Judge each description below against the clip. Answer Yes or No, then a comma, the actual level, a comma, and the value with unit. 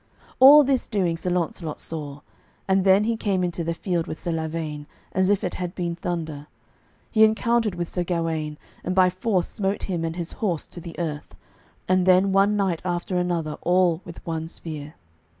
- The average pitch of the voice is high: No, medium, 175 Hz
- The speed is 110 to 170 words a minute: No, average, 185 wpm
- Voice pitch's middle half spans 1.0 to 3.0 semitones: Yes, narrow, 2.6 semitones